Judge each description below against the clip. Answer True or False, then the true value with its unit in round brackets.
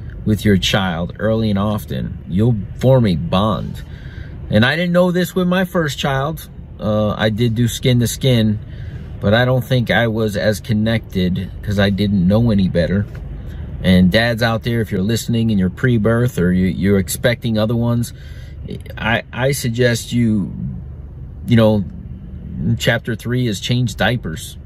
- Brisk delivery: False (165 wpm)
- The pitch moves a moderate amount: True (3.6 semitones)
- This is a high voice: False (110 Hz)